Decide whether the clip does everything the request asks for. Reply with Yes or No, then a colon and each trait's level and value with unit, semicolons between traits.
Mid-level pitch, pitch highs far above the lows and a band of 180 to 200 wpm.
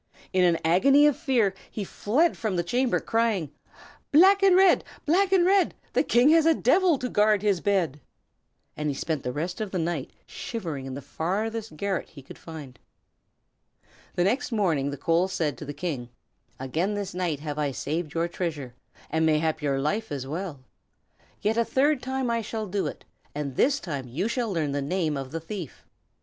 Yes: medium, 180 Hz; wide, 7.4 semitones; average, 190 wpm